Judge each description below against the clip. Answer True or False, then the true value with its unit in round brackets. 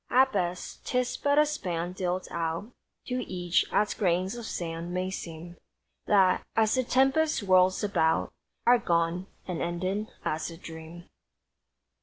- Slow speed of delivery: False (145 wpm)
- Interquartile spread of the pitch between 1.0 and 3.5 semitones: False (4.2 semitones)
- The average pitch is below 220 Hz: True (185 Hz)